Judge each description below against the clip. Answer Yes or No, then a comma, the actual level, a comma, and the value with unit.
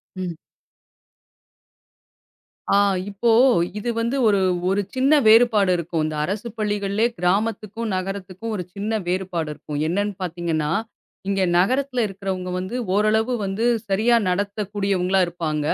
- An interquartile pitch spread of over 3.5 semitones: No, average, 3.1 semitones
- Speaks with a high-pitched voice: Yes, high, 200 Hz